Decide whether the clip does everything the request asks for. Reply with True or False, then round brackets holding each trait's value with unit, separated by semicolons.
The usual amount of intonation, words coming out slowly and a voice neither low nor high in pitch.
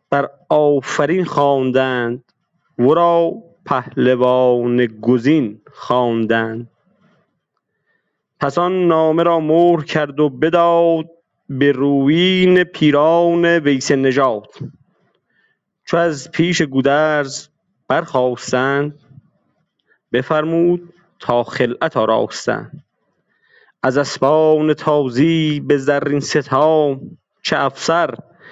True (4.0 semitones; 80 wpm; 150 Hz)